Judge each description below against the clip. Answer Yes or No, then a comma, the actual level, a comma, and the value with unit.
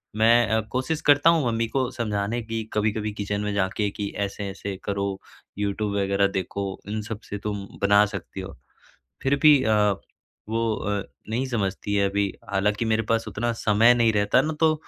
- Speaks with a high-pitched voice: No, low, 105 Hz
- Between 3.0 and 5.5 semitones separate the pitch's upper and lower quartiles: No, narrow, 2.5 semitones